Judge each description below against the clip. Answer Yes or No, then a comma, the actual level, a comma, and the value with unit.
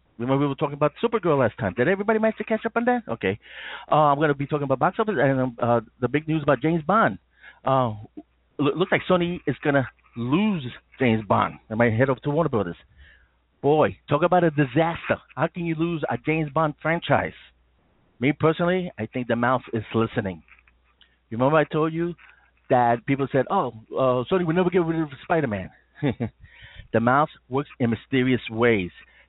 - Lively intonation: Yes, wide, 5.8 semitones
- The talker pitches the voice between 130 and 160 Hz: Yes, medium, 140 Hz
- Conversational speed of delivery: Yes, average, 195 wpm